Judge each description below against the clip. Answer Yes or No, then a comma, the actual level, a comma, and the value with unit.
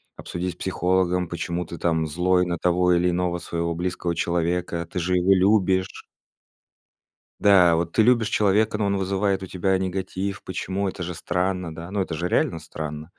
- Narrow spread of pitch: Yes, narrow, 1.8 semitones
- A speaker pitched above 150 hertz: No, very low, 90 Hz